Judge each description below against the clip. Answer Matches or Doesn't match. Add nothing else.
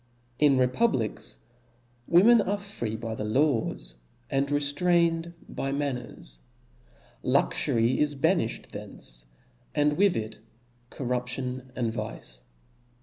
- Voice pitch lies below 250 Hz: Matches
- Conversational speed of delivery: Doesn't match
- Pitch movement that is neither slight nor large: Doesn't match